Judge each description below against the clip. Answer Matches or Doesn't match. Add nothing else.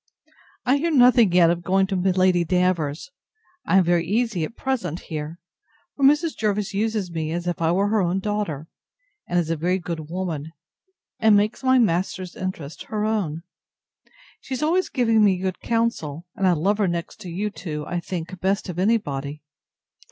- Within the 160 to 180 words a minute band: Doesn't match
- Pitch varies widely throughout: Doesn't match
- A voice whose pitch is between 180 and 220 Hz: Matches